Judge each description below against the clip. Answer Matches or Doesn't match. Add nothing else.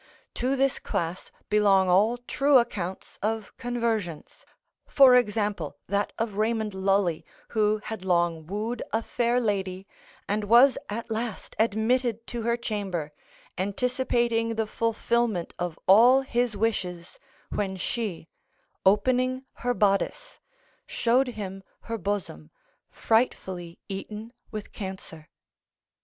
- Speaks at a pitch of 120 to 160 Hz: Doesn't match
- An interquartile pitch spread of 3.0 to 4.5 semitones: Matches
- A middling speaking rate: Doesn't match